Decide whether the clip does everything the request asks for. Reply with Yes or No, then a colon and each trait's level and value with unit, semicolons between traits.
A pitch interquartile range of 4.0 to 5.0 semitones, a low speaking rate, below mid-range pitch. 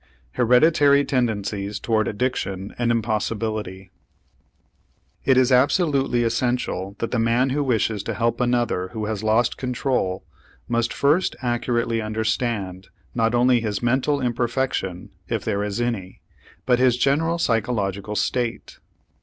No: average, 2.9 semitones; slow, 125 wpm; low, 120 Hz